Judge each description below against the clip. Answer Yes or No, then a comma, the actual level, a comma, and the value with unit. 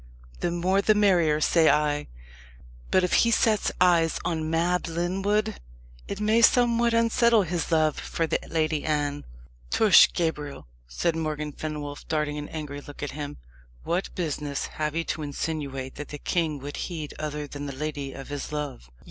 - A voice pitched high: No, medium, 155 Hz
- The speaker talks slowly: No, average, 165 wpm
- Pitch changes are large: No, average, 3.4 semitones